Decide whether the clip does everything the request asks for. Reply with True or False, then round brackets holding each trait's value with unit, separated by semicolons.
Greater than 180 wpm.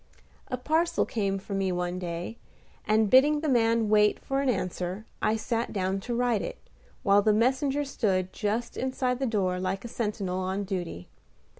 False (175 wpm)